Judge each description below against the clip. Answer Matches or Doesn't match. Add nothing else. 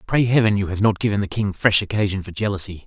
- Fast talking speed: Matches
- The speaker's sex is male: Matches